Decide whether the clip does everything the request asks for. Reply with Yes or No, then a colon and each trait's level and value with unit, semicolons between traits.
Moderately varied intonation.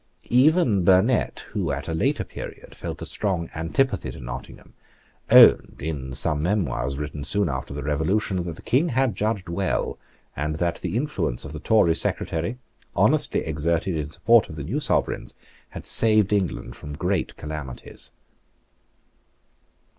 No: wide, 6.0 semitones